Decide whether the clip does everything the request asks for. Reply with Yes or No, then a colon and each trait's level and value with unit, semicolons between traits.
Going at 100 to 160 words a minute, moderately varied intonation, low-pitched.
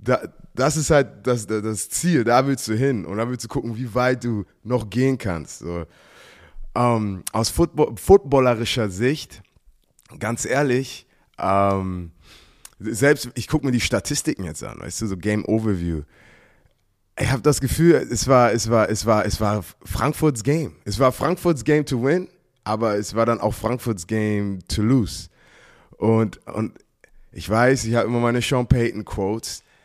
No: average, 170 wpm; average, 3.9 semitones; low, 115 Hz